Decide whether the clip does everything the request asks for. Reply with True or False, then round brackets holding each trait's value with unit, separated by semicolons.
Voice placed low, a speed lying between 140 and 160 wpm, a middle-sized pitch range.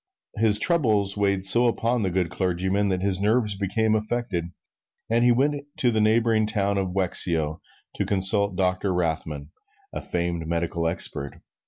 True (100 Hz; 155 wpm; 3.6 semitones)